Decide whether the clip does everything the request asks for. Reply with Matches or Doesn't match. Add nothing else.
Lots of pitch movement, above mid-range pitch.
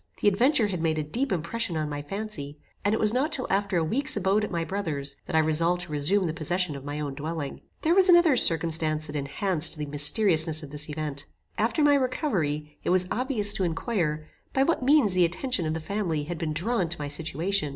Doesn't match